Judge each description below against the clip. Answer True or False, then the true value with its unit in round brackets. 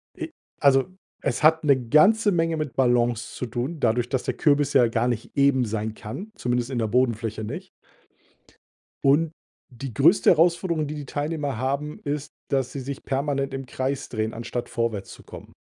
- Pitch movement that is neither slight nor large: True (3.8 semitones)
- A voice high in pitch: False (135 Hz)